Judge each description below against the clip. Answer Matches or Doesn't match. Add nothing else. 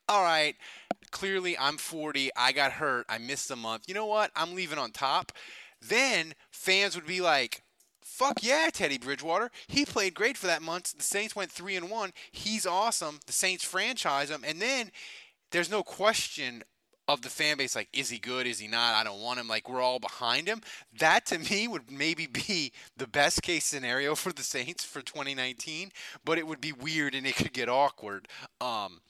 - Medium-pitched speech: Matches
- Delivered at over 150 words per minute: Matches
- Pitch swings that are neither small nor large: Doesn't match